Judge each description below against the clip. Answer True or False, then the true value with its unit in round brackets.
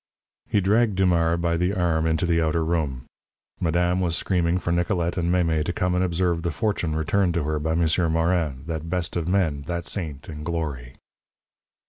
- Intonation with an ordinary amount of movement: False (1.9 semitones)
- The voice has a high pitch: False (85 Hz)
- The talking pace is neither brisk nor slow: True (185 wpm)